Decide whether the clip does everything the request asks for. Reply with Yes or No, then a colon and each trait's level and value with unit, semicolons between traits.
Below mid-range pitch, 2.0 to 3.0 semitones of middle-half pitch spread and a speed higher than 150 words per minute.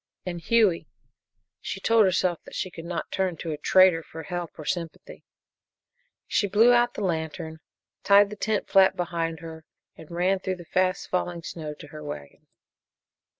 No: medium, 175 Hz; average, 2.7 semitones; average, 170 wpm